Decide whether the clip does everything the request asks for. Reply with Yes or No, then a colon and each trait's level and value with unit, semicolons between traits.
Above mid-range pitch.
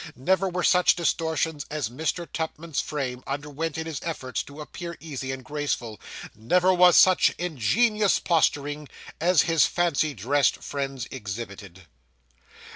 No: medium, 150 Hz